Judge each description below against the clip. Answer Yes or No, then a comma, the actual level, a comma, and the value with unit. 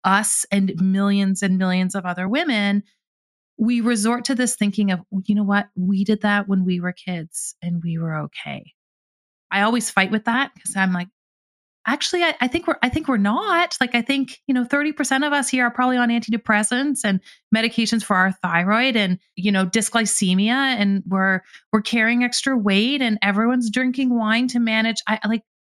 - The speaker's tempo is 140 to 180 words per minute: No, average, 190 wpm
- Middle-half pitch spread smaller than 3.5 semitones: No, average, 4.0 semitones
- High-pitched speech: Yes, high, 220 Hz